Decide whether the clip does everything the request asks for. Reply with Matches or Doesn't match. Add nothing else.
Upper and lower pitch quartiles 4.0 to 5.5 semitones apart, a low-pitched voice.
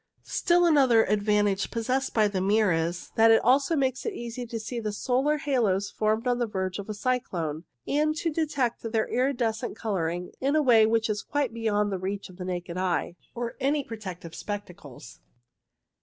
Doesn't match